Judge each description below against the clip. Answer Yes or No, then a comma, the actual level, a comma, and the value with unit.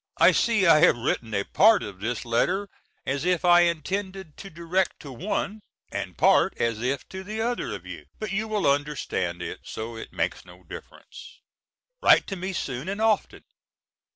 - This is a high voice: No, medium, 170 Hz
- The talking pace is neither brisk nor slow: Yes, average, 180 wpm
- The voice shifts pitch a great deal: Yes, wide, 8.5 semitones